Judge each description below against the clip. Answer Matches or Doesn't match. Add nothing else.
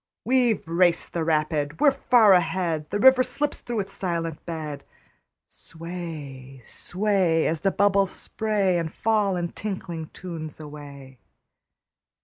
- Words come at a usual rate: Doesn't match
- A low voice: Doesn't match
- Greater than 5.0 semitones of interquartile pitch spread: Doesn't match